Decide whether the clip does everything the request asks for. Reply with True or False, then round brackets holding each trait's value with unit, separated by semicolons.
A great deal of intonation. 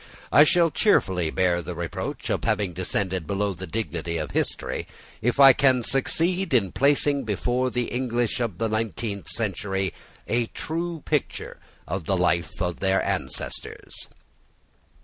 True (5.8 semitones)